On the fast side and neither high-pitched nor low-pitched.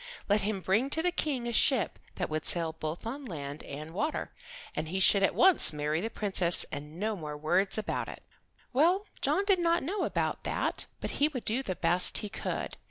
No: fast, 210 wpm; high, 200 Hz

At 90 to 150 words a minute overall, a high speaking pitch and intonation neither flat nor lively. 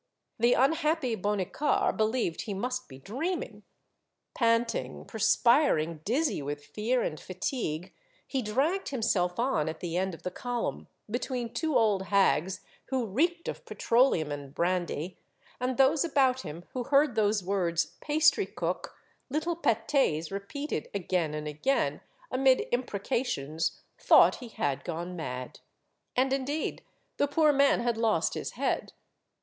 No: average, 140 wpm; high, 230 Hz; wide, 7.2 semitones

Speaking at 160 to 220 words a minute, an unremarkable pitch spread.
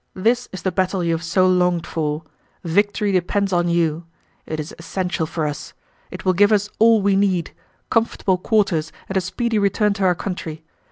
Yes: average, 185 wpm; average, 3.2 semitones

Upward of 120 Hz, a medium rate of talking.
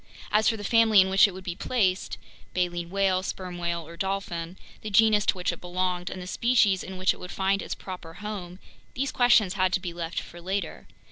No: medium, 185 Hz; fast, 220 wpm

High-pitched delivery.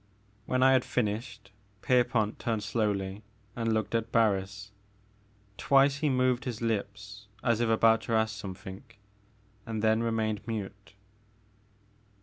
No: low, 110 Hz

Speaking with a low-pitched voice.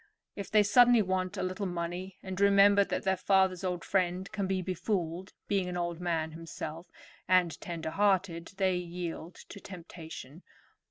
No: medium, 185 Hz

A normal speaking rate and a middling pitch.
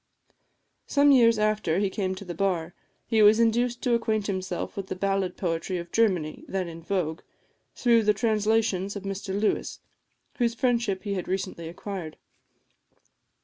No: average, 155 wpm; high, 200 Hz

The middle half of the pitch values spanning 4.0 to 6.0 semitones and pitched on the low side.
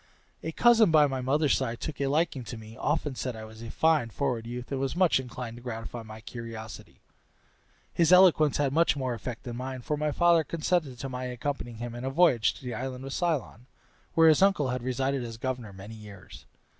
Yes: average, 4.3 semitones; low, 130 Hz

